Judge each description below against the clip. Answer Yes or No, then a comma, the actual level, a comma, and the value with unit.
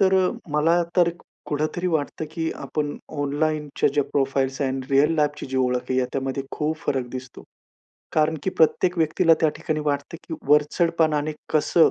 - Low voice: No, medium, 150 Hz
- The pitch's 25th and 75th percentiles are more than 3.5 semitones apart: No, average, 2.7 semitones